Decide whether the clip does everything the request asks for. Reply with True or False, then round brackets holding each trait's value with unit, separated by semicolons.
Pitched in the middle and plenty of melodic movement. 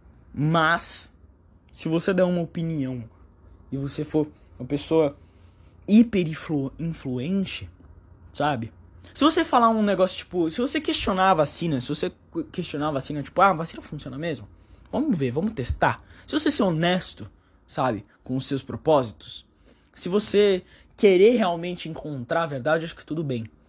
True (150 Hz; 8.8 semitones)